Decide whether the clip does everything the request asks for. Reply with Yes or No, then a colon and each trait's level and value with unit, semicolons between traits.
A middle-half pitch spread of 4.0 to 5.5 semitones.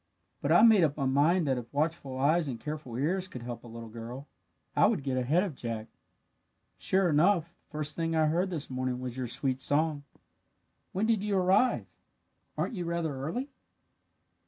Yes: average, 5.2 semitones